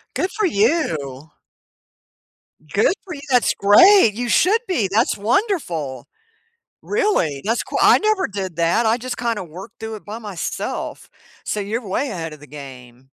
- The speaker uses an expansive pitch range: Yes, wide, 7.6 semitones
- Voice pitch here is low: No, high, 210 Hz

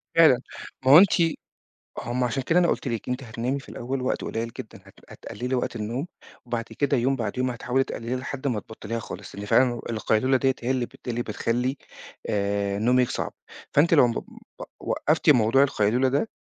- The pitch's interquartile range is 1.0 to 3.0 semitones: Yes, narrow, 2.6 semitones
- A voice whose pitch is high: No, low, 125 Hz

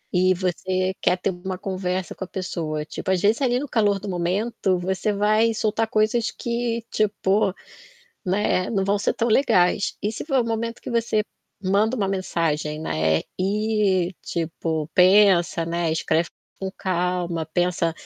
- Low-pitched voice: No, high, 190 Hz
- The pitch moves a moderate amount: Yes, average, 3.3 semitones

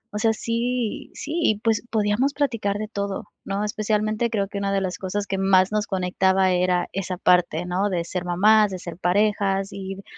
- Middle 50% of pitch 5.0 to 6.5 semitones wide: No, narrow, 2.4 semitones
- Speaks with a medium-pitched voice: No, high, 200 Hz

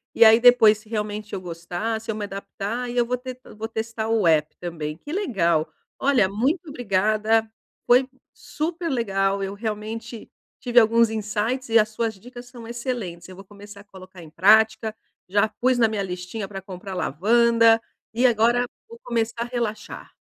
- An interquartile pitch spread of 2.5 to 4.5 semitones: Yes, average, 3.3 semitones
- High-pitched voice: Yes, high, 220 Hz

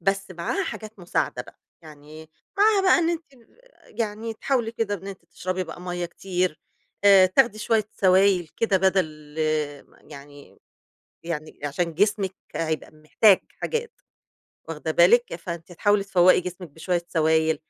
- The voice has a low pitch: No, medium, 185 Hz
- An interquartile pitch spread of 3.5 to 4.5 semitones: Yes, average, 4.2 semitones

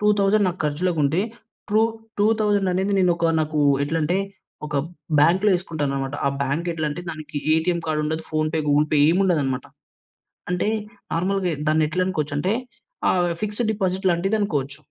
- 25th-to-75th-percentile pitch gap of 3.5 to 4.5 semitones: Yes, average, 3.9 semitones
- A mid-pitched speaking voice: Yes, medium, 170 Hz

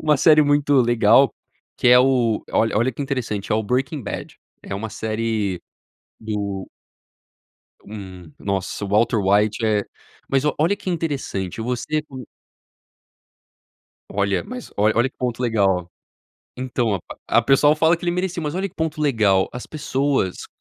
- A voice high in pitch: No, low, 120 Hz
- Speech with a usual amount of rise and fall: No, wide, 5.9 semitones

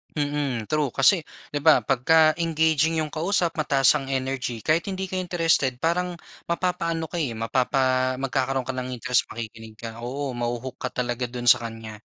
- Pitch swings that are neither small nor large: Yes, average, 4.7 semitones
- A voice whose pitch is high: No, low, 135 Hz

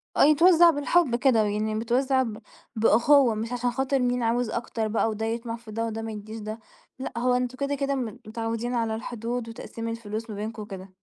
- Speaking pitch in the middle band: No, high, 230 Hz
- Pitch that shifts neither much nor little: No, narrow, 2.3 semitones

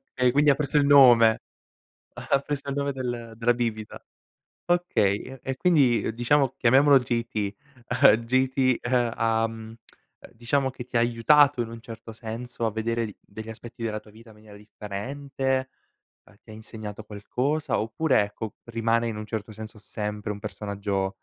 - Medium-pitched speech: No, low, 115 Hz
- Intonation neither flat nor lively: Yes, average, 3.3 semitones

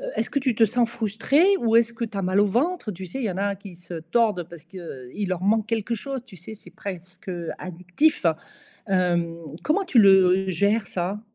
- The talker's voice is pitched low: No, high, 200 Hz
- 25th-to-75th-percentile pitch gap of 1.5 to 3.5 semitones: No, average, 4.1 semitones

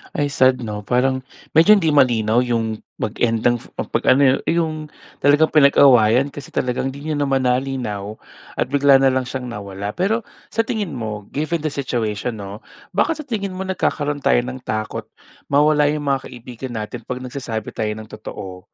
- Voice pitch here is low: Yes, low, 130 Hz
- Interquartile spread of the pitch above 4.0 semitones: Yes, average, 4.6 semitones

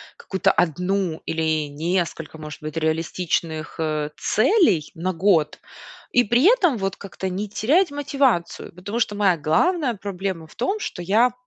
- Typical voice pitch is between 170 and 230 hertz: Yes, medium, 185 Hz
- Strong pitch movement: Yes, wide, 6.5 semitones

